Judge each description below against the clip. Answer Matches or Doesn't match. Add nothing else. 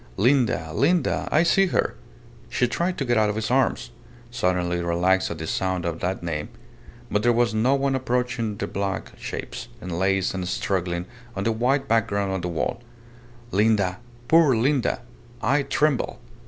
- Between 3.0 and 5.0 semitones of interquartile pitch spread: Doesn't match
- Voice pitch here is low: Matches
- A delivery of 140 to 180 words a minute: Matches